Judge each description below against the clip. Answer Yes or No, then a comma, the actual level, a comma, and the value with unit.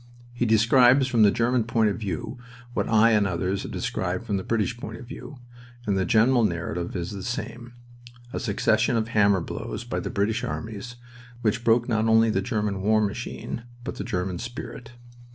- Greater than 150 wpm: Yes, average, 190 wpm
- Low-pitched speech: Yes, low, 110 Hz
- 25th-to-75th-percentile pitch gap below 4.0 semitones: Yes, average, 2.9 semitones